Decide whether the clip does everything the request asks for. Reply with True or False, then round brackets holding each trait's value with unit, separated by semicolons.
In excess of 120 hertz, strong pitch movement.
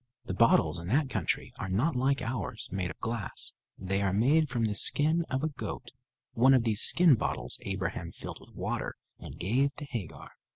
False (115 Hz; 6.1 semitones)